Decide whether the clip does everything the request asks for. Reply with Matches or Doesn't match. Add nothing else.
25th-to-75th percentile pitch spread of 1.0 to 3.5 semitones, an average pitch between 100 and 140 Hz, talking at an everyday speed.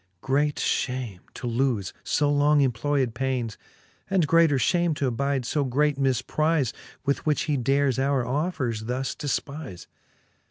Doesn't match